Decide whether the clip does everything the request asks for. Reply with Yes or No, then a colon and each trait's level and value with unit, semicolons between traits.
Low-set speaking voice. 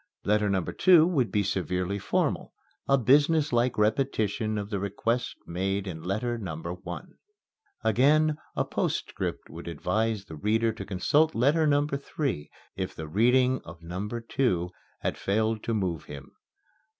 Yes: low, 110 Hz